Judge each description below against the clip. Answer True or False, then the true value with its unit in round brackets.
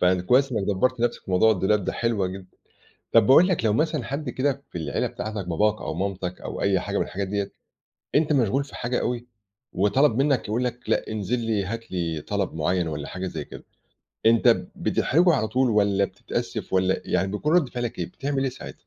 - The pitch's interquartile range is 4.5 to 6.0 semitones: True (5.1 semitones)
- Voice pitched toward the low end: True (110 Hz)